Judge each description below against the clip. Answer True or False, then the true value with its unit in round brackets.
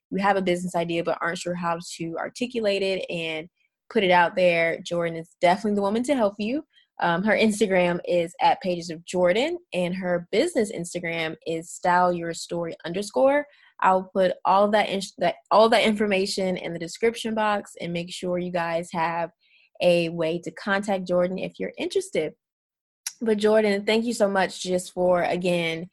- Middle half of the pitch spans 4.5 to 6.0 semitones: False (3.2 semitones)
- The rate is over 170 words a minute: True (180 wpm)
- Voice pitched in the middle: True (180 Hz)